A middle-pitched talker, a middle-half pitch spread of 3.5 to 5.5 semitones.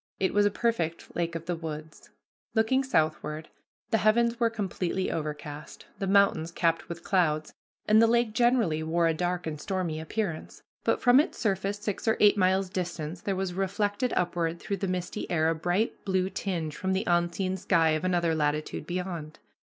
Yes: medium, 180 Hz; average, 3.9 semitones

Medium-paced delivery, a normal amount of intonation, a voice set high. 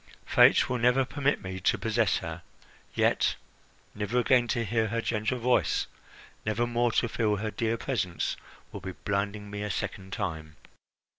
No: average, 160 wpm; average, 3.0 semitones; low, 110 Hz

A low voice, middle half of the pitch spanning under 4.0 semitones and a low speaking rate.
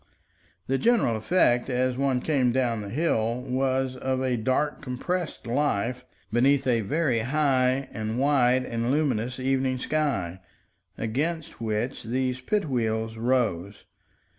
Yes: low, 130 Hz; average, 2.8 semitones; slow, 130 wpm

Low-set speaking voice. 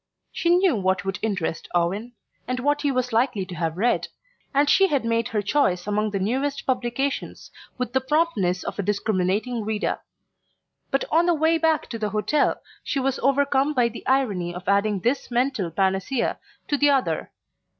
No: high, 240 Hz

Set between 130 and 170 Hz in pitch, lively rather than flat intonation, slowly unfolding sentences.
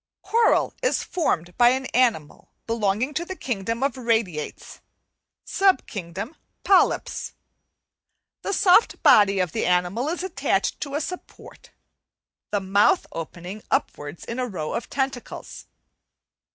No: high, 230 Hz; wide, 7.4 semitones; slow, 125 wpm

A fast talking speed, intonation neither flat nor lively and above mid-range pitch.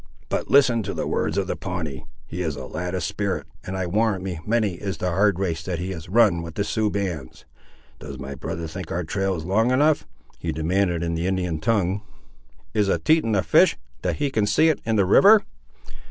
No: fast, 220 wpm; average, 3.9 semitones; very low, 95 Hz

